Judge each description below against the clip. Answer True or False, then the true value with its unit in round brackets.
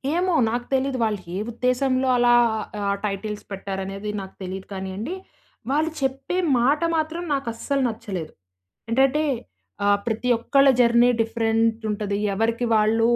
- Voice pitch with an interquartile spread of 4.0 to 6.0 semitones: True (4.3 semitones)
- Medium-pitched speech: False (230 Hz)